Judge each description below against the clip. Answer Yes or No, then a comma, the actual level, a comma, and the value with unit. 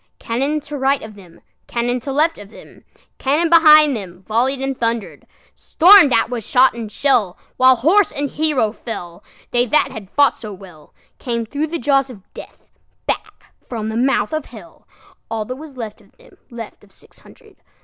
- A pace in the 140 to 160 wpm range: Yes, average, 150 wpm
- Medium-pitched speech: No, very high, 250 Hz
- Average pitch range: Yes, average, 4.7 semitones